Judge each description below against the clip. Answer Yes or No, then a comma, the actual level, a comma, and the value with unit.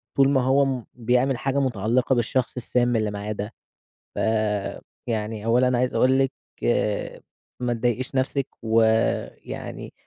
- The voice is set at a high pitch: No, low, 125 Hz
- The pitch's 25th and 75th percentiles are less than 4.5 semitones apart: Yes, average, 2.7 semitones